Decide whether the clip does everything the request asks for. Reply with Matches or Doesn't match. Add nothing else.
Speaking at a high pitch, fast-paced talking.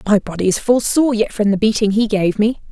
Matches